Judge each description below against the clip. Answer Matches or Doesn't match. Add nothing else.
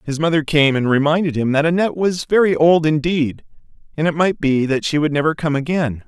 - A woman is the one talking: Doesn't match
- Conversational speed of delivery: Doesn't match